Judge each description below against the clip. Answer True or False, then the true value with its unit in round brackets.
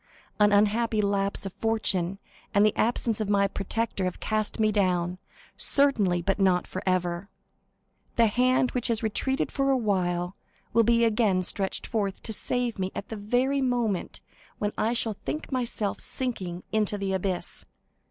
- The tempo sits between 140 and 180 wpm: True (160 wpm)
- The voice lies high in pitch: True (210 Hz)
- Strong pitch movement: False (3.3 semitones)